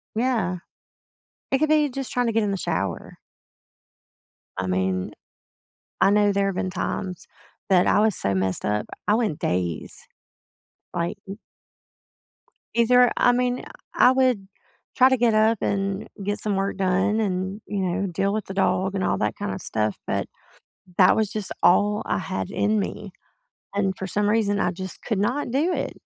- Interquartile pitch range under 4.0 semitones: Yes, average, 3.4 semitones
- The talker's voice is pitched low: No, high, 200 Hz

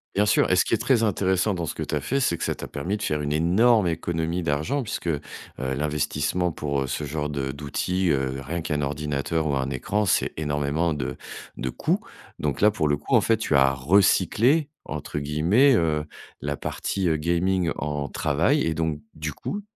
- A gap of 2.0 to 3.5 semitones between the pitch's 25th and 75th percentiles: No, average, 4.3 semitones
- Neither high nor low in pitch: No, very low, 80 Hz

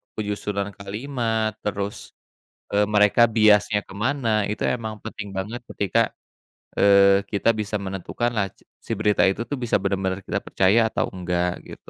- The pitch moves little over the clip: Yes, narrow, 2.0 semitones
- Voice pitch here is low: Yes, low, 105 Hz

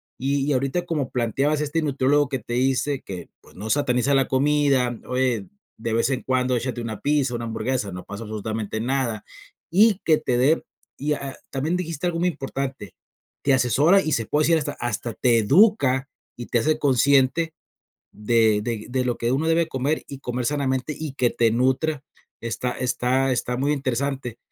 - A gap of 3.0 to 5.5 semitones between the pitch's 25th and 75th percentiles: Yes, average, 3.4 semitones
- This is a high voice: No, low, 130 Hz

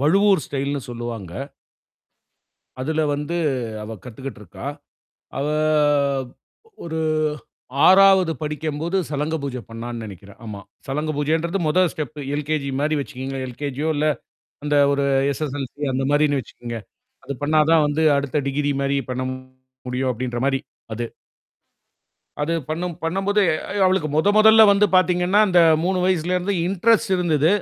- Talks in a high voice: No, medium, 150 Hz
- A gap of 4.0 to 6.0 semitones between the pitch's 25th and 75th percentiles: Yes, average, 4.4 semitones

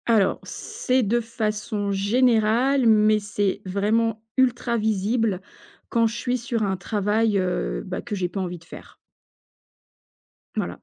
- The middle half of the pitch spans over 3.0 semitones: No, average, 2.7 semitones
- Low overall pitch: No, high, 215 Hz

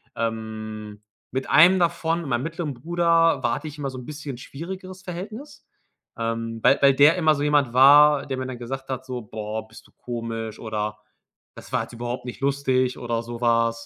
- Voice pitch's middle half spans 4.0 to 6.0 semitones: Yes, average, 4.7 semitones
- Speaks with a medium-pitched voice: No, low, 130 Hz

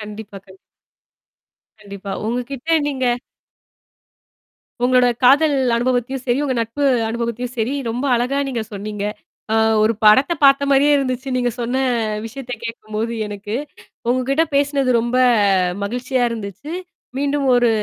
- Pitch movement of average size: Yes, average, 3.5 semitones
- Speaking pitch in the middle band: No, high, 245 Hz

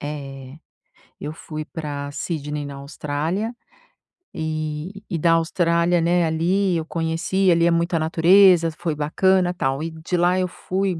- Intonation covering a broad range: No, average, 2.8 semitones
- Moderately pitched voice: Yes, medium, 165 Hz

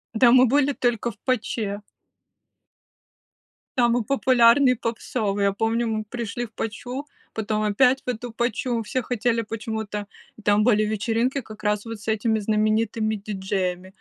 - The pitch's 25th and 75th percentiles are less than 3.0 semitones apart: Yes, narrow, 2.5 semitones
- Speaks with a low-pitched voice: No, high, 225 Hz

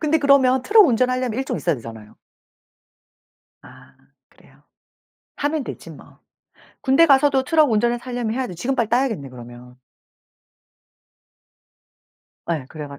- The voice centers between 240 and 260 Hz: Yes, high, 245 Hz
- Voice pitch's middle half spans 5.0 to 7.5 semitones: No, wide, 8.9 semitones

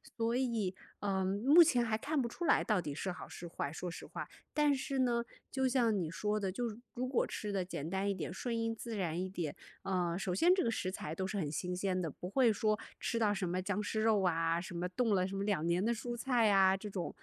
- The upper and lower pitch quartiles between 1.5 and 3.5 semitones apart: No, average, 4.3 semitones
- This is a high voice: Yes, high, 200 Hz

